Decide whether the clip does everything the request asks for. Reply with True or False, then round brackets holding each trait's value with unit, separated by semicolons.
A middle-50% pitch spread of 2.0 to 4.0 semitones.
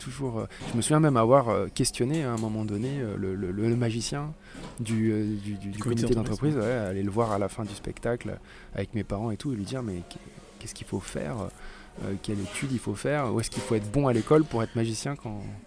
True (3.7 semitones)